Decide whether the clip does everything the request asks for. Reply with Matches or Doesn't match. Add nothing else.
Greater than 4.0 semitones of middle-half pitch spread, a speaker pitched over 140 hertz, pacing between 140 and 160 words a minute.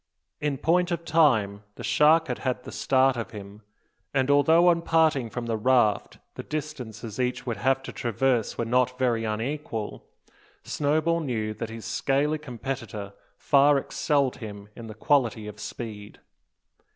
Doesn't match